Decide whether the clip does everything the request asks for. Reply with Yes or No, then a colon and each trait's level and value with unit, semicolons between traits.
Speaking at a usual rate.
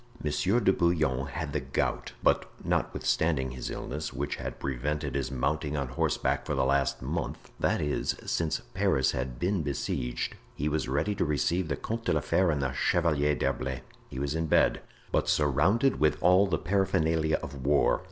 Yes: average, 175 wpm